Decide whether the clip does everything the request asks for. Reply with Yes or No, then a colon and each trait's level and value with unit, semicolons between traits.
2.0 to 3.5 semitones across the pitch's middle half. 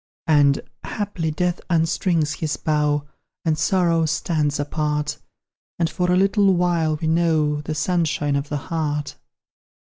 Yes: narrow, 2.5 semitones